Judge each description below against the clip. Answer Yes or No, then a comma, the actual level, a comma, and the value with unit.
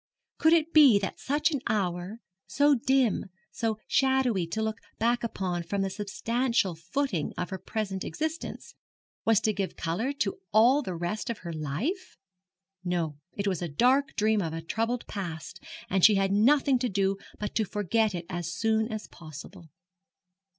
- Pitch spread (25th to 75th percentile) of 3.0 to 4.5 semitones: No, average, 5.2 semitones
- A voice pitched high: Yes, high, 210 Hz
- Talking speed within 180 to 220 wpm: No, average, 170 wpm